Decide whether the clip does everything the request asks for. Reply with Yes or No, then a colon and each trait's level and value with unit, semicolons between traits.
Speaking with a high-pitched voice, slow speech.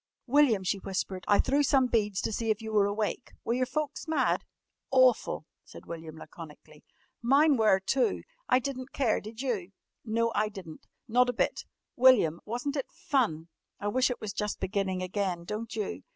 No: high, 220 Hz; average, 180 wpm